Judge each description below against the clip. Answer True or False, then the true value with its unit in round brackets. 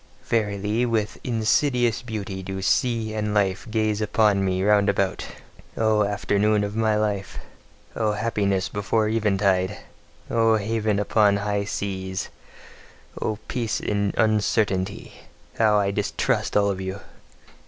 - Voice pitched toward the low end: True (105 Hz)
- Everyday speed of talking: False (125 wpm)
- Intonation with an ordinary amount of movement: False (1.6 semitones)